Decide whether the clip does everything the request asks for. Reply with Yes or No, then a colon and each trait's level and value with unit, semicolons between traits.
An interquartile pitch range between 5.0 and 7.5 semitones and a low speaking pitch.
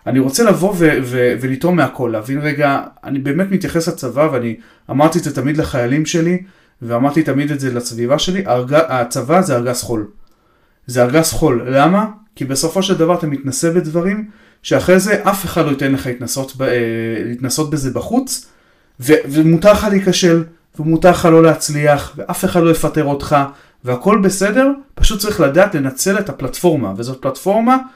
No: average, 5.3 semitones; medium, 155 Hz